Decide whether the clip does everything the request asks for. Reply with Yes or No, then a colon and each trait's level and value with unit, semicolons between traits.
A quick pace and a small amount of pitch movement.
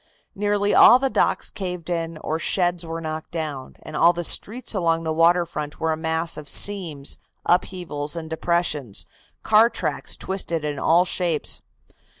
No: average, 160 wpm; narrow, 2.3 semitones